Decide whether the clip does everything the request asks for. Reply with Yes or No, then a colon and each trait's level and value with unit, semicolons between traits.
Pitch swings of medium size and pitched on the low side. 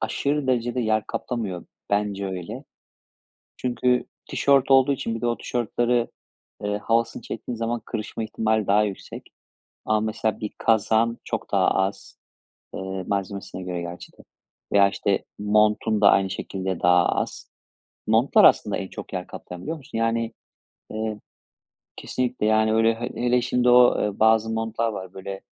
Yes: average, 3.0 semitones; low, 110 Hz